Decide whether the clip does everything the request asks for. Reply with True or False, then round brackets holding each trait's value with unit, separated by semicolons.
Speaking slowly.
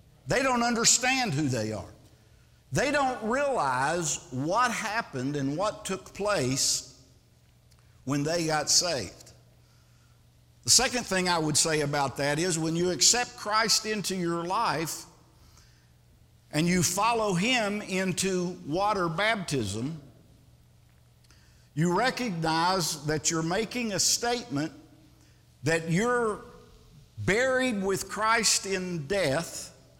True (110 wpm)